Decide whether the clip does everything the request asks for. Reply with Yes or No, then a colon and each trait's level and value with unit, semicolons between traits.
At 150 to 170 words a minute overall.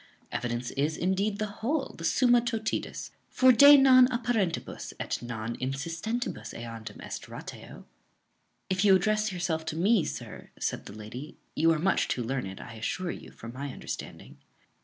Yes: average, 160 wpm